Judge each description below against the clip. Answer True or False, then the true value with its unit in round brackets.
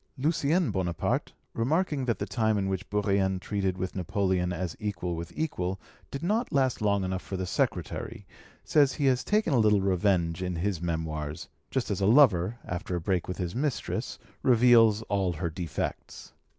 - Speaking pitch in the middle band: False (100 Hz)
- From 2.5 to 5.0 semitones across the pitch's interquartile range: False (5.4 semitones)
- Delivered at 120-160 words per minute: False (175 wpm)